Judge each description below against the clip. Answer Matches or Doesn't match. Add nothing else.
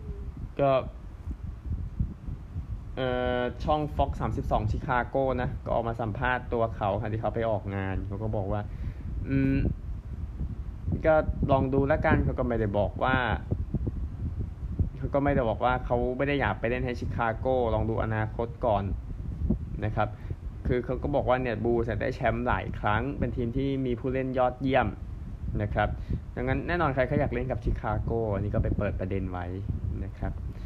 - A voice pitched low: Matches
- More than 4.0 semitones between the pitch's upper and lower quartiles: Matches